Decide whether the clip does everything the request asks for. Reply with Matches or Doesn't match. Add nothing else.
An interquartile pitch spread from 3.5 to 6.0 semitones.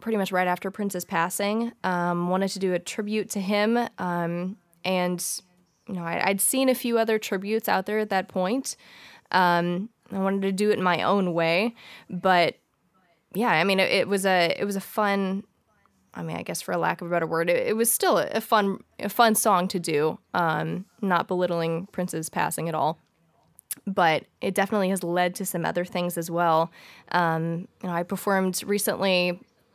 Doesn't match